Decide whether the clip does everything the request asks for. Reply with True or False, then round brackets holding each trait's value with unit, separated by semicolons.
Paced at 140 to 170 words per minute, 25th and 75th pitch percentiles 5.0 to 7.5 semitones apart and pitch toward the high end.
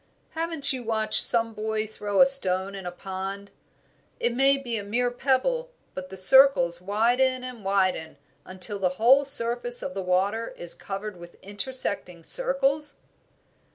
True (155 wpm; 5.3 semitones; 220 Hz)